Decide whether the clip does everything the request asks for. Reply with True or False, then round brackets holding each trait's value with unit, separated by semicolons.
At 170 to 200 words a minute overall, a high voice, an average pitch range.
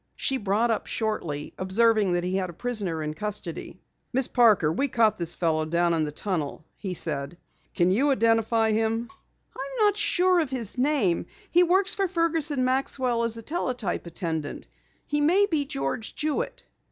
False (175 wpm; 225 Hz; 8.1 semitones)